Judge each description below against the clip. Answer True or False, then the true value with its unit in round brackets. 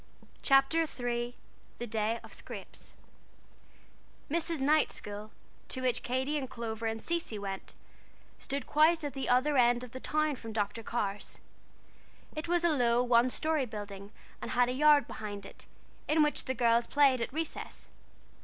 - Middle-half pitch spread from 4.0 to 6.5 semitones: True (4.5 semitones)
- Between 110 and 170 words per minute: True (160 wpm)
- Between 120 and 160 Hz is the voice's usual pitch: False (250 Hz)